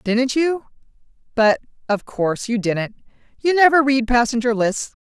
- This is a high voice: Yes, high, 245 Hz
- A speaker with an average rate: No, slow, 120 wpm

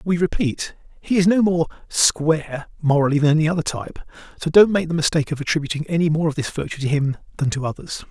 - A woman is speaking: No, male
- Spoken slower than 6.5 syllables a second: No, 6.6 syllables/s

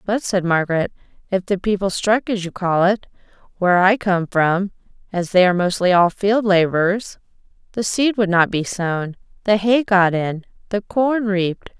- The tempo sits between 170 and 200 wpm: Yes, average, 180 wpm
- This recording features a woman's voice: Yes, female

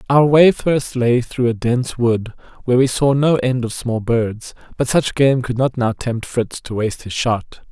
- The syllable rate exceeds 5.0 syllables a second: No, 4.5 syllables/s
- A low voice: Yes, low, 125 Hz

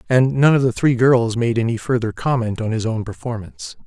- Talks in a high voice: No, low, 120 Hz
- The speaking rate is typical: No, fast, 215 wpm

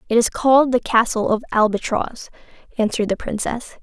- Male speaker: No, female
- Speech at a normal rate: Yes, average, 155 wpm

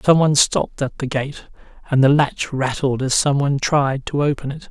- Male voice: Yes, male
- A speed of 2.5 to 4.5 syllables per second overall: No, 5.3 syllables/s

